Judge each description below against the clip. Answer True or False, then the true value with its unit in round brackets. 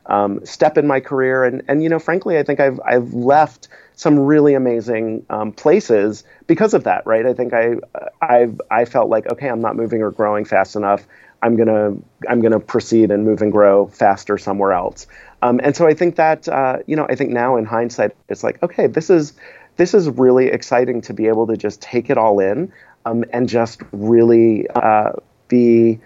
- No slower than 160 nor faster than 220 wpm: True (205 wpm)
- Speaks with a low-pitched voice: True (120 Hz)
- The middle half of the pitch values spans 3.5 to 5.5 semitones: True (3.8 semitones)